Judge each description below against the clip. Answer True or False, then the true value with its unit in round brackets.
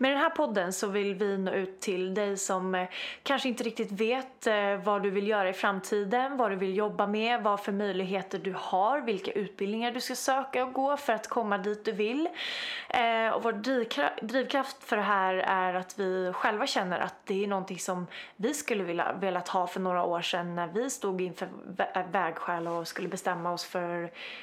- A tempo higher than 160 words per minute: True (195 wpm)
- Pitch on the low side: False (205 Hz)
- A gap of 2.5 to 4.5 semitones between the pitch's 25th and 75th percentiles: True (4.2 semitones)